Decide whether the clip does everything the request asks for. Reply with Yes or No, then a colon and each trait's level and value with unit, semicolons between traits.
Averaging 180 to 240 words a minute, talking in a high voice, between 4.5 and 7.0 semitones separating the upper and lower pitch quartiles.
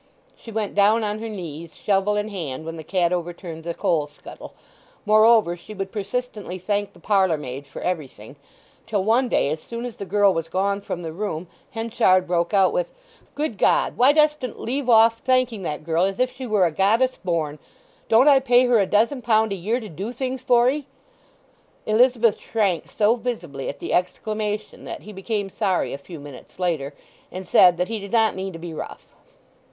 Yes: average, 200 wpm; high, 205 Hz; average, 4.8 semitones